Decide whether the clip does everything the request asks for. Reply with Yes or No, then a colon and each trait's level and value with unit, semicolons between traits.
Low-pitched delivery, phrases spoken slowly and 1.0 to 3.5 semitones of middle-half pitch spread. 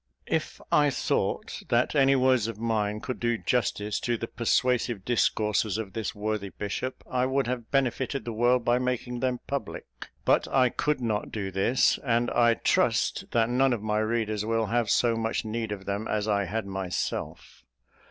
No: low, 115 Hz; average, 180 wpm; average, 2.7 semitones